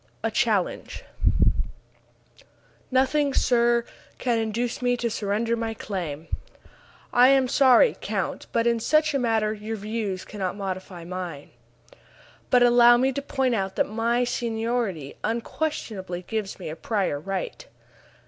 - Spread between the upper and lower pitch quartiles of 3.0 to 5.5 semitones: Yes, average, 3.9 semitones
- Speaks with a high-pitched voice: Yes, high, 225 Hz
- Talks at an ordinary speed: No, slow, 130 wpm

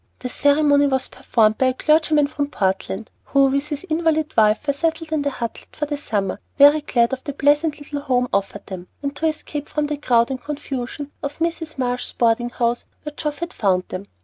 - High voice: Yes, very high, 285 Hz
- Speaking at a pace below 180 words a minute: No, fast, 205 wpm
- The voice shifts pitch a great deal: No, average, 3.7 semitones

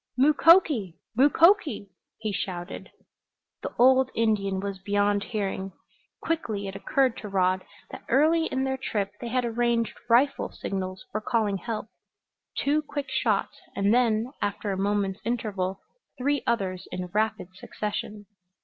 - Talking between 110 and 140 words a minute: Yes, slow, 135 wpm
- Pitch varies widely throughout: No, average, 4.7 semitones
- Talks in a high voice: Yes, high, 215 Hz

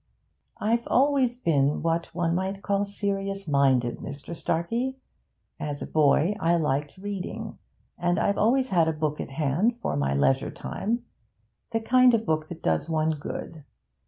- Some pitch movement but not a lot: No, wide, 5.9 semitones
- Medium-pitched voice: Yes, medium, 170 Hz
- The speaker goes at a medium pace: Yes, average, 160 wpm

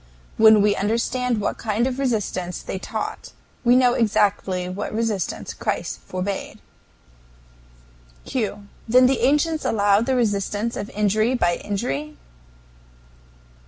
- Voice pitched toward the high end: Yes, high, 215 Hz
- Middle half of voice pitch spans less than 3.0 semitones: No, average, 3.4 semitones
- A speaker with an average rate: No, slow, 120 wpm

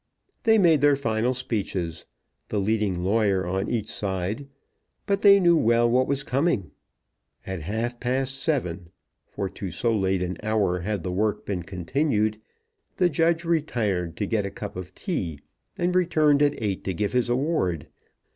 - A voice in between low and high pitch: No, low, 110 Hz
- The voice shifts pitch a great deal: Yes, wide, 6.8 semitones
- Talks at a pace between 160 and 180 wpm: Yes, average, 165 wpm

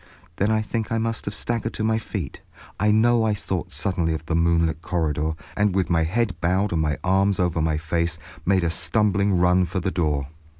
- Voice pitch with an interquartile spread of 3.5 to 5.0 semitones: Yes, average, 4.3 semitones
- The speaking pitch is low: Yes, very low, 90 Hz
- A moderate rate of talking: No, fast, 210 wpm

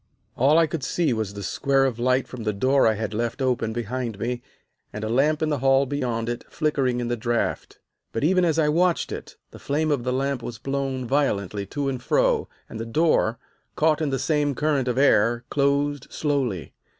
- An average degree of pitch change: Yes, average, 3.7 semitones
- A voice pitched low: Yes, low, 130 Hz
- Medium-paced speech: No, fast, 210 wpm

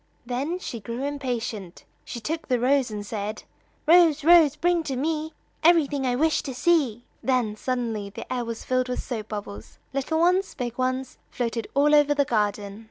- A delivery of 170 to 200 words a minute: Yes, average, 175 wpm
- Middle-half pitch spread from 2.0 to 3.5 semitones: No, average, 4.6 semitones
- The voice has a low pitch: No, very high, 255 Hz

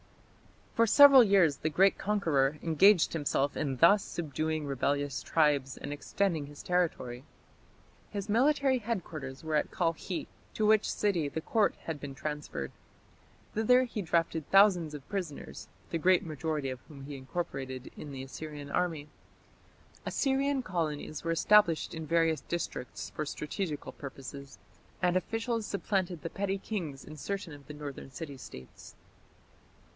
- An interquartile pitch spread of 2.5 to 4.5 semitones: No, wide, 5.4 semitones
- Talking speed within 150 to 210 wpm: No, average, 140 wpm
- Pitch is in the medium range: Yes, medium, 160 Hz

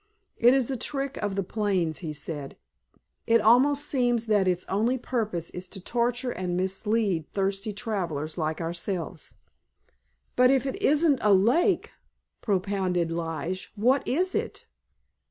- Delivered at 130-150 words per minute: Yes, average, 140 wpm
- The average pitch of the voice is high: Yes, high, 205 Hz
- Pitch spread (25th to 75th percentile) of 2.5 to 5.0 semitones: No, wide, 5.5 semitones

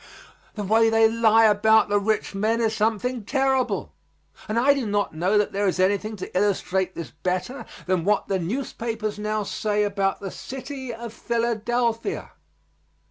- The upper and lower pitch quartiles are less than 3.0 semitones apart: Yes, narrow, 2.5 semitones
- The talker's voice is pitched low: No, high, 215 Hz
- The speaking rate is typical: Yes, average, 160 wpm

